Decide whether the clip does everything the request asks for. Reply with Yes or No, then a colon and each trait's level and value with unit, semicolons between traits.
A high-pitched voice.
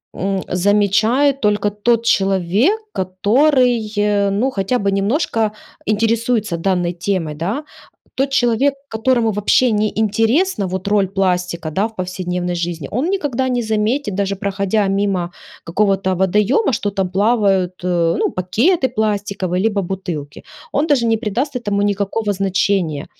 Yes: high, 205 Hz